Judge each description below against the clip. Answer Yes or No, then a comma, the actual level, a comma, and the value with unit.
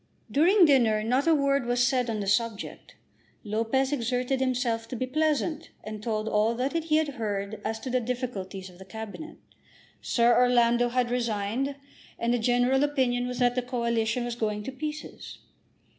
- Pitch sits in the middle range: No, high, 245 Hz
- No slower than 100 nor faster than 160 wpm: No, average, 175 wpm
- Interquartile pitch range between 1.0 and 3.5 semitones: Yes, average, 3.0 semitones